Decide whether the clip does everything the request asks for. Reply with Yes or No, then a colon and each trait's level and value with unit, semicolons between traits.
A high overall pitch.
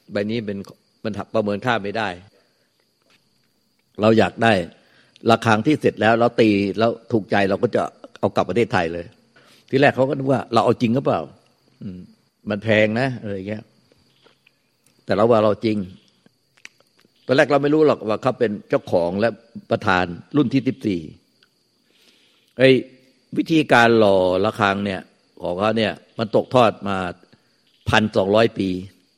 No: low, 110 Hz